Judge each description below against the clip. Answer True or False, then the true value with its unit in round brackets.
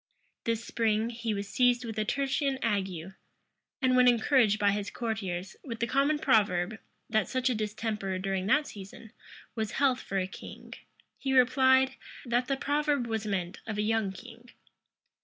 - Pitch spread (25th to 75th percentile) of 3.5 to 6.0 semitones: True (3.9 semitones)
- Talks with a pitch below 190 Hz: False (225 Hz)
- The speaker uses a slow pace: False (165 wpm)